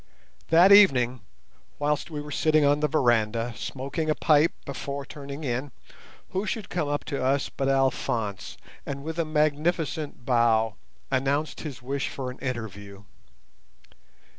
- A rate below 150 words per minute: Yes, average, 140 wpm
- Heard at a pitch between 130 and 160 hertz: Yes, medium, 140 Hz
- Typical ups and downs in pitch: Yes, average, 3.6 semitones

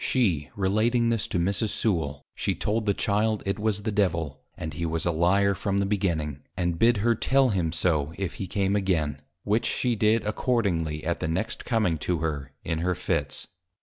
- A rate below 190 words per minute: No, average, 195 wpm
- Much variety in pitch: No, average, 4.7 semitones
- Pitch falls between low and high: No, very low, 95 Hz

